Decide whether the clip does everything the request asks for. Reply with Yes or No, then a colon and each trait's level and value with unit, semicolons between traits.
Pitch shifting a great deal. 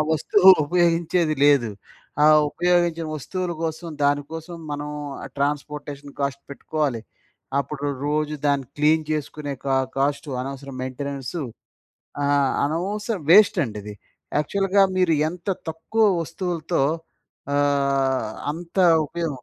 No: average, 3.5 semitones